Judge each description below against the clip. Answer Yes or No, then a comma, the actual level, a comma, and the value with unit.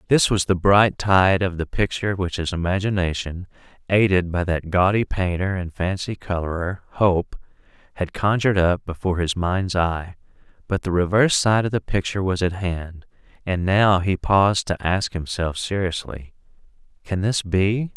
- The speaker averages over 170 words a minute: No, average, 160 wpm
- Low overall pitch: Yes, very low, 95 Hz